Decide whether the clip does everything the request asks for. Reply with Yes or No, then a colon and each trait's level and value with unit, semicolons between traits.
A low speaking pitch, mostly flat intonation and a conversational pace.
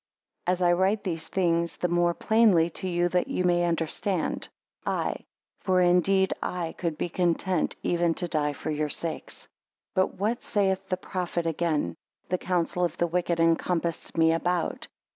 No: medium, 175 Hz; narrow, 1.8 semitones; average, 160 wpm